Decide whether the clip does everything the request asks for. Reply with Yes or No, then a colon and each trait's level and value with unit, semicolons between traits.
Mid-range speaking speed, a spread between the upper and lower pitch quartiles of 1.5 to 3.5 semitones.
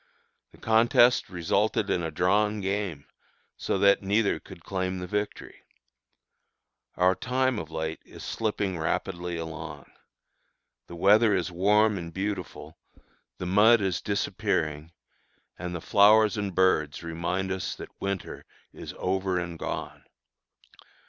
No: slow, 125 wpm; average, 3.2 semitones